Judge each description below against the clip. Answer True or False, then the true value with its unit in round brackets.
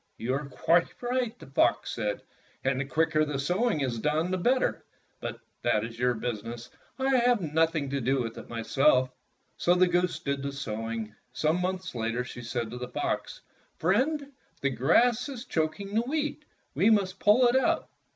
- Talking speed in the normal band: True (180 wpm)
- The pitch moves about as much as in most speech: False (8.8 semitones)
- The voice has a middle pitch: True (155 Hz)